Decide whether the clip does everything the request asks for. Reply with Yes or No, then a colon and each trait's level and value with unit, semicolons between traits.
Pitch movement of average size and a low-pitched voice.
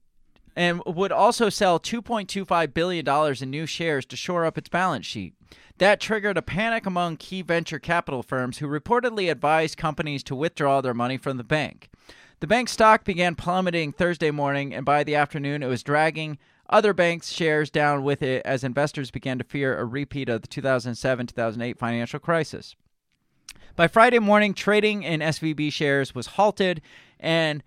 No: average, 4.5 semitones; medium, 155 Hz